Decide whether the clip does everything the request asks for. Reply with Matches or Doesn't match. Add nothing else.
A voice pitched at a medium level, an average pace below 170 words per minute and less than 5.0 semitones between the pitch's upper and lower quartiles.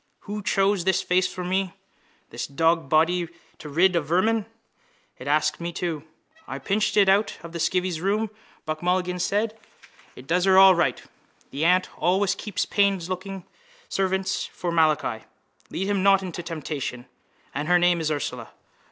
Matches